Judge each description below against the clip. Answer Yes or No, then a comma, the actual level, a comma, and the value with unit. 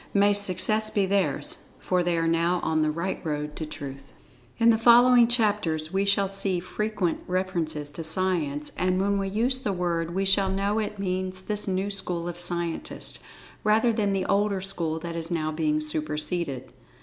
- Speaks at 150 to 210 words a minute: Yes, average, 175 wpm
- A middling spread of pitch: Yes, average, 3.5 semitones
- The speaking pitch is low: No, medium, 185 Hz